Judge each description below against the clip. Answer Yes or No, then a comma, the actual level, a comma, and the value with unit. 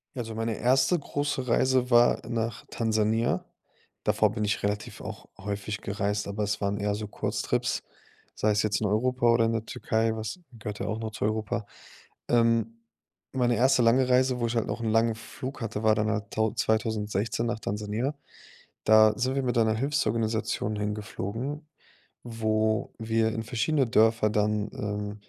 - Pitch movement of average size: No, narrow, 2.1 semitones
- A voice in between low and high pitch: No, low, 110 Hz